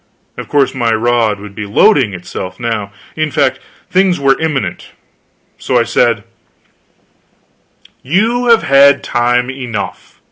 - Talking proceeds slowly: Yes, slow, 130 wpm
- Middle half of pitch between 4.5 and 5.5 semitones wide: Yes, average, 5.2 semitones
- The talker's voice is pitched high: No, low, 130 Hz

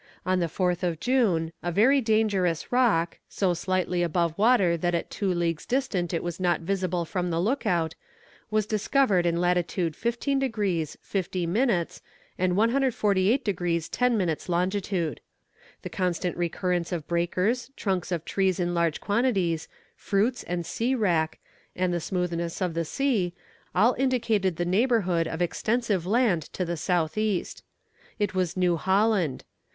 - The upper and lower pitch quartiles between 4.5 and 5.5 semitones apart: No, average, 3.9 semitones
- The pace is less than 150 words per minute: No, average, 155 wpm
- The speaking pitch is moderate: Yes, medium, 180 Hz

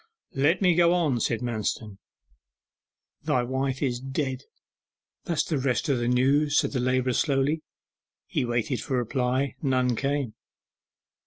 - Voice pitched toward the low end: Yes, low, 130 Hz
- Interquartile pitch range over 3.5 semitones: No, narrow, 2.5 semitones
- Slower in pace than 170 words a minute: Yes, average, 145 wpm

